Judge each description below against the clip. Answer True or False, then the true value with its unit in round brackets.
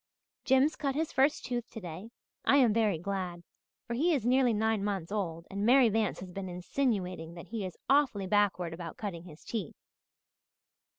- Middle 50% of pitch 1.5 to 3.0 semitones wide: False (5.4 semitones)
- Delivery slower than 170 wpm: False (175 wpm)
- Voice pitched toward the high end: True (205 Hz)